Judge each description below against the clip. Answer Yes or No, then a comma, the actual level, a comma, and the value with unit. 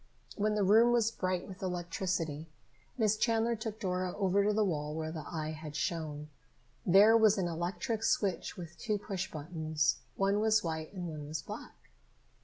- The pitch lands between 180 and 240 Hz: Yes, medium, 185 Hz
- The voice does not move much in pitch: No, average, 4.8 semitones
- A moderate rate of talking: Yes, average, 175 wpm